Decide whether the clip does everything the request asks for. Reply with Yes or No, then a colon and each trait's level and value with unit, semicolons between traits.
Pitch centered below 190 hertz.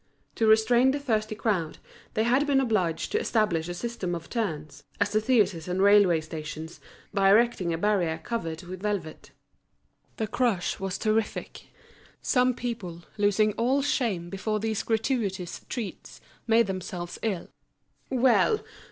No: high, 210 Hz